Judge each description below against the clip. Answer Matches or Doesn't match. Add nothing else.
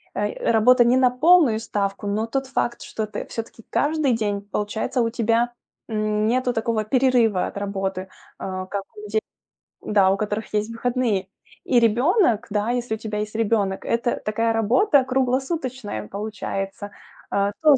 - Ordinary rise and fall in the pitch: Matches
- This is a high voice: Matches